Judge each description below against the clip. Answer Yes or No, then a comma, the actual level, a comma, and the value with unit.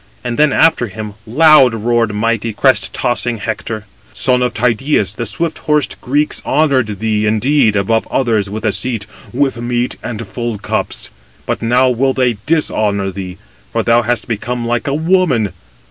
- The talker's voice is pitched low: Yes, low, 120 Hz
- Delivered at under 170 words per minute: Yes, average, 160 wpm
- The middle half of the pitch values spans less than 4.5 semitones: Yes, average, 3.4 semitones